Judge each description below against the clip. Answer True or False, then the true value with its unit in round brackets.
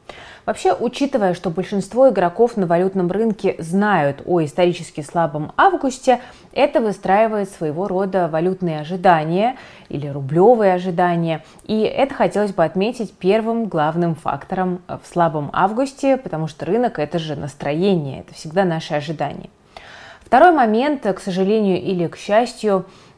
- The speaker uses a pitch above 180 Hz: True (190 Hz)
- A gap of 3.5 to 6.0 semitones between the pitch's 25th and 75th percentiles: True (4.7 semitones)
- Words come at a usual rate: True (130 wpm)